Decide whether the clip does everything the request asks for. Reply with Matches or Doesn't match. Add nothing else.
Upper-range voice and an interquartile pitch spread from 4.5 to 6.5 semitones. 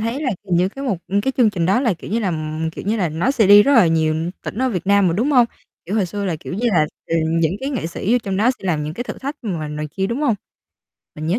Matches